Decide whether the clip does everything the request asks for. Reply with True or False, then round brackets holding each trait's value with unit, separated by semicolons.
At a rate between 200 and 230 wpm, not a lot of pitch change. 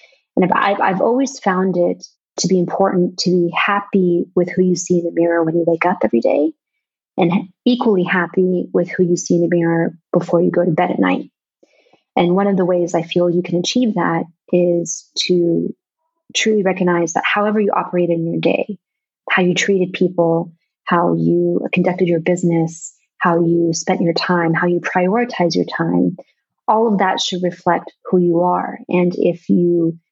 False (190 wpm; 1.7 semitones)